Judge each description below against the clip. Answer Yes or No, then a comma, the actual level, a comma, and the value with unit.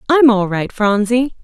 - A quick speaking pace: No, average, 165 wpm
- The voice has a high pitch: Yes, high, 230 Hz